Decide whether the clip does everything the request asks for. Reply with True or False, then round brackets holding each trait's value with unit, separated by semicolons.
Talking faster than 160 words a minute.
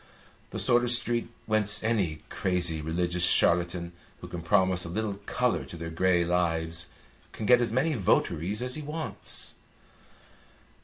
False (150 wpm)